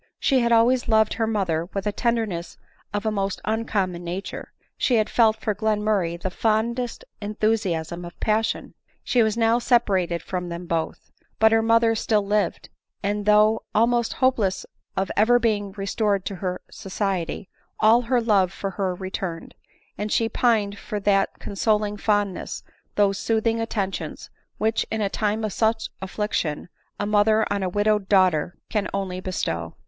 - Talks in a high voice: Yes, high, 210 Hz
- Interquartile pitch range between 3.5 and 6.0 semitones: No, average, 2.7 semitones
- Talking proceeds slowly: No, average, 165 wpm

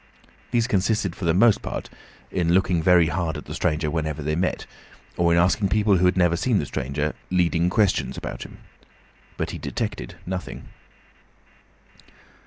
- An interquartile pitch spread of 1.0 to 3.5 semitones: Yes, average, 2.7 semitones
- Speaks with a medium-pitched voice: No, very low, 90 Hz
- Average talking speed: Yes, average, 165 wpm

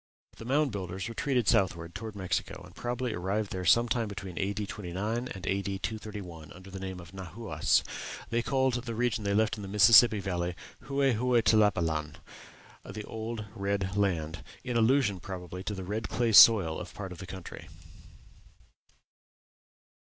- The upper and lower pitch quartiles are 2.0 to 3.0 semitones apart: No, average, 3.6 semitones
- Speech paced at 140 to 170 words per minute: Yes, average, 165 wpm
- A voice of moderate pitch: No, low, 100 Hz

